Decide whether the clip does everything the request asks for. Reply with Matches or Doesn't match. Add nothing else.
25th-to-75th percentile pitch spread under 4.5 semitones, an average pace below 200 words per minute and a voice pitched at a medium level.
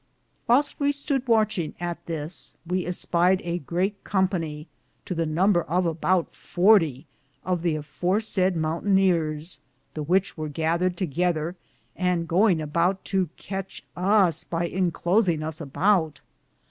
Matches